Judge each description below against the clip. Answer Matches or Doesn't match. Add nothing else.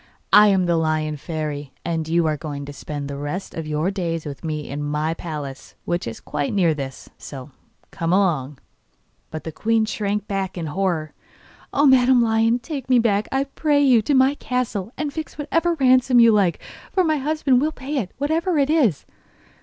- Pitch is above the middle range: Matches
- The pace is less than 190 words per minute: Doesn't match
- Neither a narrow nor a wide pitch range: Doesn't match